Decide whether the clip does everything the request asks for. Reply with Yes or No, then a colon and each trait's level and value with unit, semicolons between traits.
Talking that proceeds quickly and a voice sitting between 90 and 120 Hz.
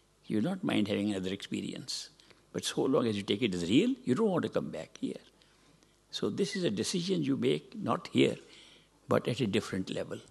Yes: fast, 215 wpm; low, 115 Hz